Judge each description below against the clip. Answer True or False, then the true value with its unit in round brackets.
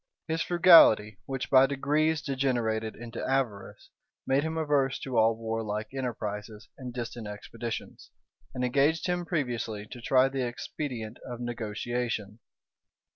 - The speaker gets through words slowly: True (130 wpm)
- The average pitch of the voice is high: False (125 Hz)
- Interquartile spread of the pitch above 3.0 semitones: True (3.6 semitones)